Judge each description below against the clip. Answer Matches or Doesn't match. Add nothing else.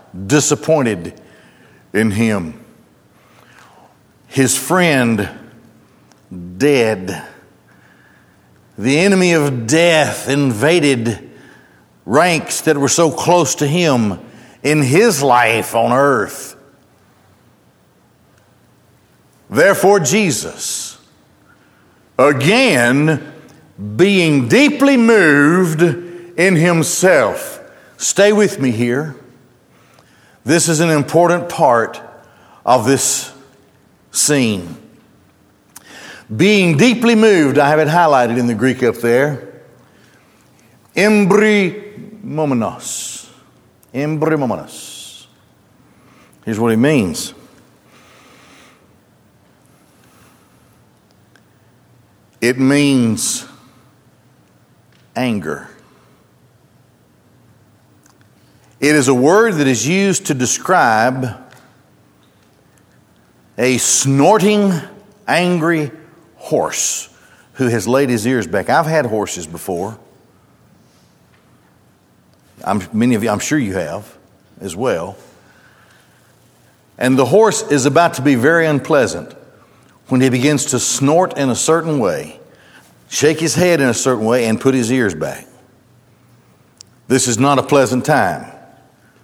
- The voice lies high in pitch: Doesn't match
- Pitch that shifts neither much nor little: Doesn't match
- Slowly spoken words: Matches